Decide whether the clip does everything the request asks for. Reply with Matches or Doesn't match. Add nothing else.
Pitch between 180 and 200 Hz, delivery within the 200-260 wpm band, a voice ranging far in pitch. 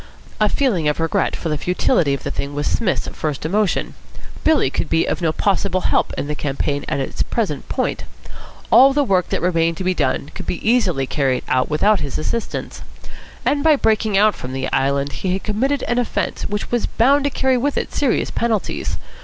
Matches